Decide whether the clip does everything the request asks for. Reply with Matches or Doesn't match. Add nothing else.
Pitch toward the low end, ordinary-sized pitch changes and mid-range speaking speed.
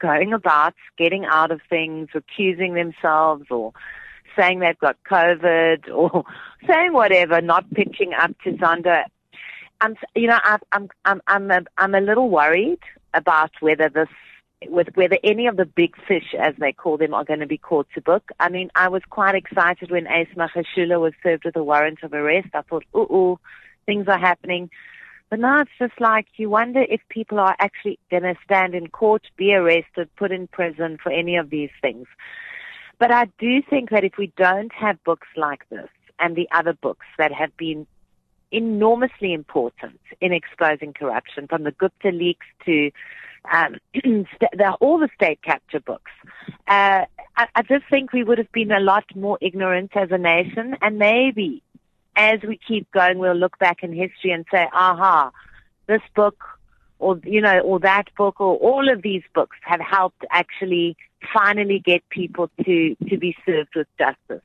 Doesn't match